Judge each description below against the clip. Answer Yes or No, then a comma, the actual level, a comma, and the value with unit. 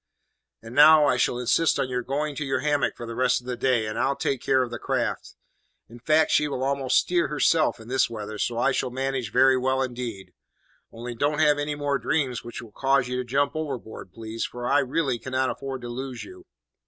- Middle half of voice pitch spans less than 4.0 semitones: Yes, average, 2.9 semitones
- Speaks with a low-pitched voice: Yes, low, 130 Hz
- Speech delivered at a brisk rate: Yes, fast, 225 wpm